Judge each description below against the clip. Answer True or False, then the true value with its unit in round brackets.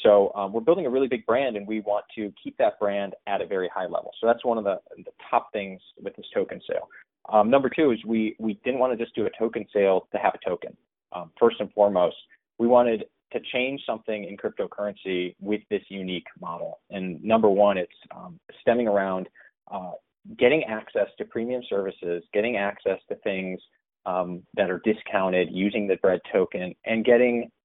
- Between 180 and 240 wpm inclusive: True (200 wpm)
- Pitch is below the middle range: True (105 Hz)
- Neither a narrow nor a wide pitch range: True (3.4 semitones)